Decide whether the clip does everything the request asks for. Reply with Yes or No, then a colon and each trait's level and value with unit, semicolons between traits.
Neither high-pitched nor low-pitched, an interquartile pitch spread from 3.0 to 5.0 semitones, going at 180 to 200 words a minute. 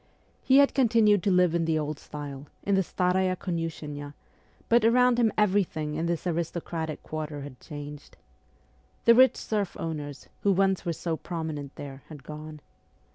No: medium, 165 Hz; average, 4.6 semitones; average, 160 wpm